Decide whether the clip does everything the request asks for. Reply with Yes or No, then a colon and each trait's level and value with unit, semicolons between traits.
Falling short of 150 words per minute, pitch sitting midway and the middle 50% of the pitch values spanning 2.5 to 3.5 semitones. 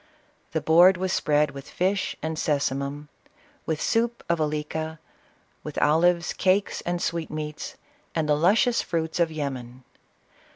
Yes: average, 140 wpm; medium, 160 Hz; average, 2.9 semitones